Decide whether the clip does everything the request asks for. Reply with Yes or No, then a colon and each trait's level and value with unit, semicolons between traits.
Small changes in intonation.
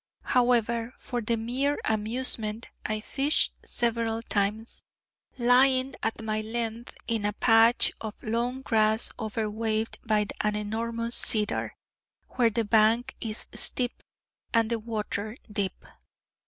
Yes: narrow, 1.8 semitones